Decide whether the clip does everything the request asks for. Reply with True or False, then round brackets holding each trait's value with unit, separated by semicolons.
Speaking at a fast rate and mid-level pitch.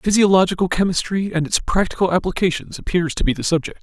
False (175 wpm; 180 Hz)